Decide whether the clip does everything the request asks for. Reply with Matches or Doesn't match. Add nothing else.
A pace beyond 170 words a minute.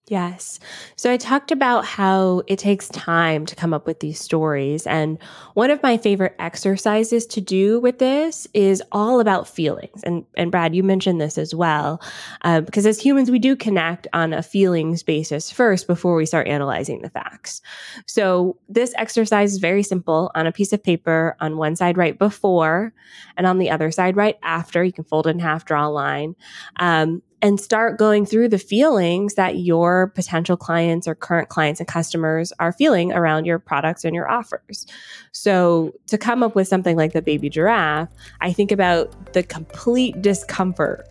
Matches